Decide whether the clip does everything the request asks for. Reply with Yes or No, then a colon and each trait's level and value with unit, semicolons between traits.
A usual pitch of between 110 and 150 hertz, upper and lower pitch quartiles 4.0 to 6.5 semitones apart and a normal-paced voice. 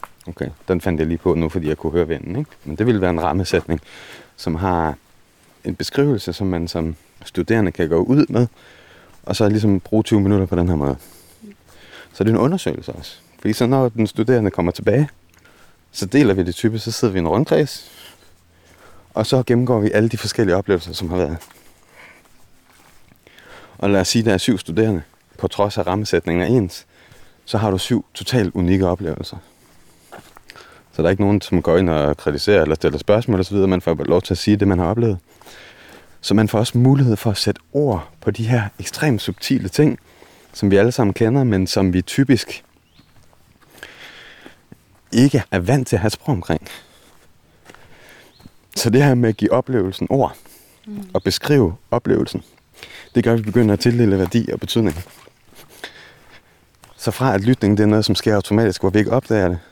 No: low, 100 Hz; average, 4.4 semitones; average, 190 wpm